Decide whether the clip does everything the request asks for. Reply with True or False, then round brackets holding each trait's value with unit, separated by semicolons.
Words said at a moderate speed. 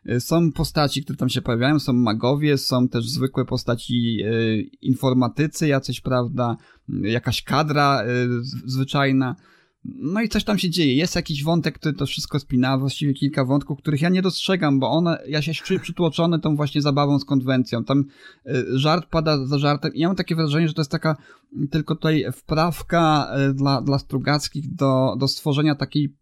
False (165 wpm)